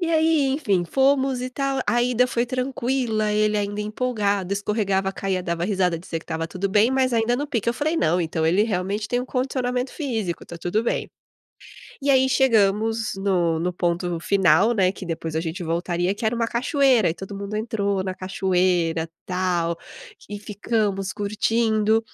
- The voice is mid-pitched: No, high, 205 Hz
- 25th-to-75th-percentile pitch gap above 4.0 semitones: Yes, average, 4.8 semitones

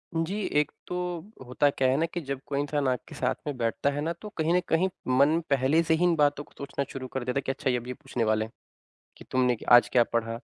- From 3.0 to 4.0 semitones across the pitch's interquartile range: Yes, average, 3.5 semitones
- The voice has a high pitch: No, medium, 140 Hz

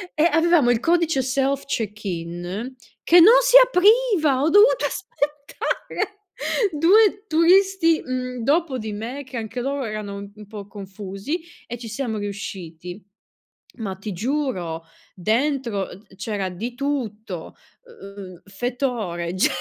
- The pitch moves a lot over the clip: Yes, wide, 7.6 semitones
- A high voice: Yes, high, 245 Hz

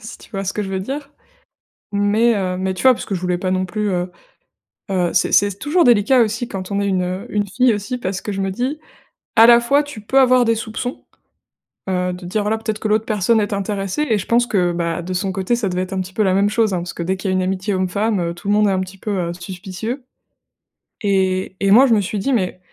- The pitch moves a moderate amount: Yes, average, 3.2 semitones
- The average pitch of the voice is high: Yes, high, 200 Hz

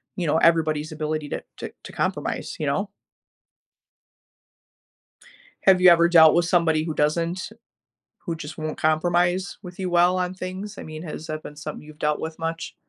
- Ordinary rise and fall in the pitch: No, narrow, 2.3 semitones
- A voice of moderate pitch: Yes, medium, 165 Hz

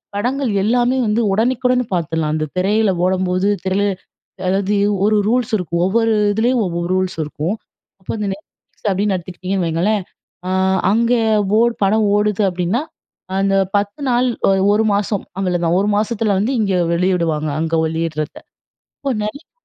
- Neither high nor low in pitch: No, high, 200 Hz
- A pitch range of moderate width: Yes, average, 3.6 semitones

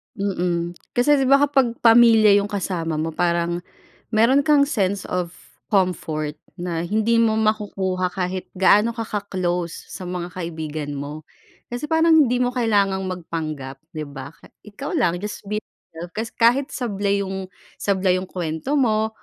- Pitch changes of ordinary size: Yes, average, 4.9 semitones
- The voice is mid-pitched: No, high, 195 Hz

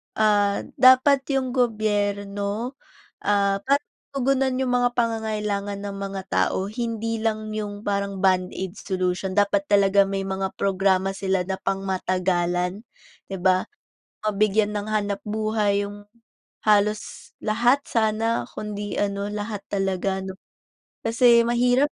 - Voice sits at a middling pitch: No, high, 205 Hz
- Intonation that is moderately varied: No, narrow, 2.3 semitones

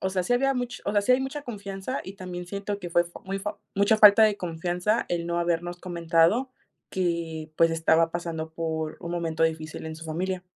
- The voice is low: No, medium, 175 Hz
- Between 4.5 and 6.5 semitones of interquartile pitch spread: No, average, 3.4 semitones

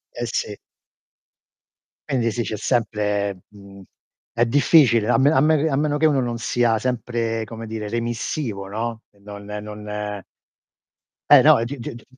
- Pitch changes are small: No, average, 3.2 semitones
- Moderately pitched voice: No, low, 115 Hz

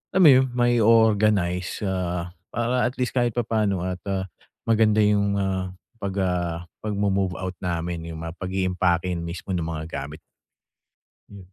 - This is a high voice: No, very low, 95 Hz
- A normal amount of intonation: Yes, average, 3.4 semitones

